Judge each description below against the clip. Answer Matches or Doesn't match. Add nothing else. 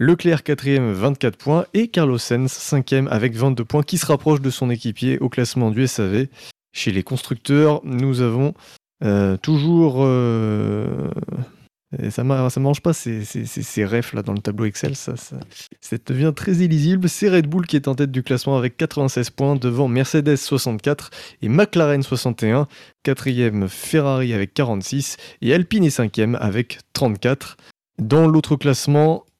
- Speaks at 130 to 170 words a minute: Matches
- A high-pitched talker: Doesn't match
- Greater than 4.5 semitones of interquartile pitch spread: Doesn't match